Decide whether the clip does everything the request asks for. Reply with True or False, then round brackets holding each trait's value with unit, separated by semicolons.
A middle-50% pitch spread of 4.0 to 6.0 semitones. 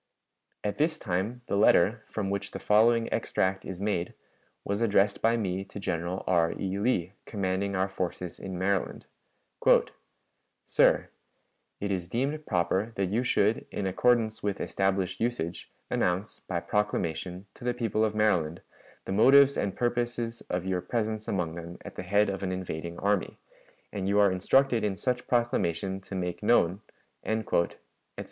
False (3.3 semitones)